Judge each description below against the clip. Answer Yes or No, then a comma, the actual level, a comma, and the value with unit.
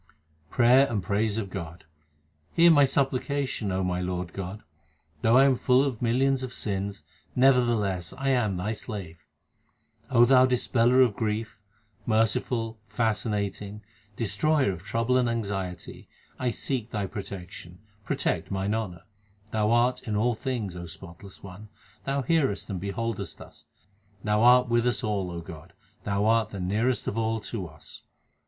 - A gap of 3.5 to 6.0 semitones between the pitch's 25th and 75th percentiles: Yes, average, 4.2 semitones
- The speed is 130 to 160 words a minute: Yes, average, 150 wpm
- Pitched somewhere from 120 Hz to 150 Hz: No, low, 110 Hz